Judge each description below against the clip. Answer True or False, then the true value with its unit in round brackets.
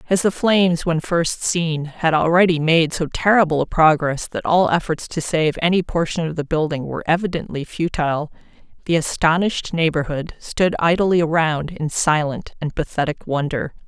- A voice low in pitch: False (160 Hz)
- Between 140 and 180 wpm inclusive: True (160 wpm)